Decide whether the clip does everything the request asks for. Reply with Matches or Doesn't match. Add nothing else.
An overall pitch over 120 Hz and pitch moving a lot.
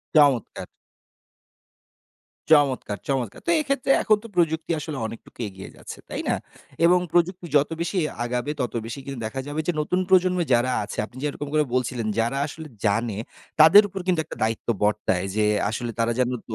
Matches